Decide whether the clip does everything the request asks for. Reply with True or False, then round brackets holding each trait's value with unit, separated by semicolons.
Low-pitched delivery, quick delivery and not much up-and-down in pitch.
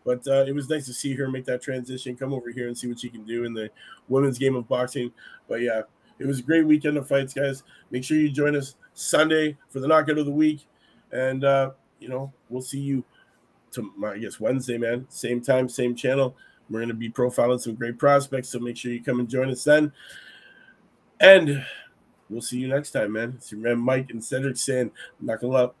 True (130 Hz; 225 wpm; 2.2 semitones)